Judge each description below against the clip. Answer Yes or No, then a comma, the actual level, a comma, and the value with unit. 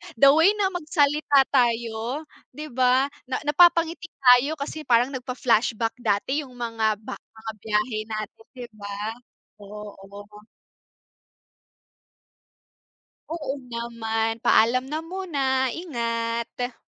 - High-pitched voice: Yes, high, 245 Hz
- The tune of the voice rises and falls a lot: No, average, 4.5 semitones